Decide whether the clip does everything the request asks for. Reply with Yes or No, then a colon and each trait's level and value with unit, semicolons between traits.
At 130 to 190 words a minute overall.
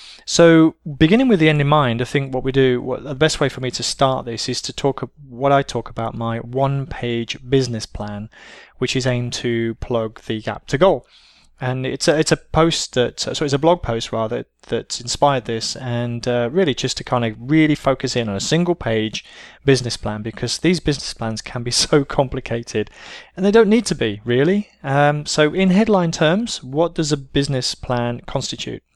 No: fast, 205 wpm